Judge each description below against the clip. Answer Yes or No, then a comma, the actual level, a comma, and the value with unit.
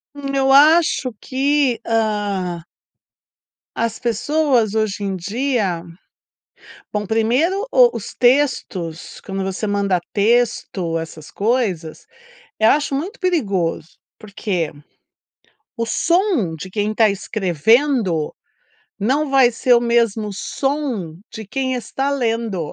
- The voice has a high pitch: Yes, high, 225 Hz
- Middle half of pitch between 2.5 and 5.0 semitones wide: No, wide, 5.6 semitones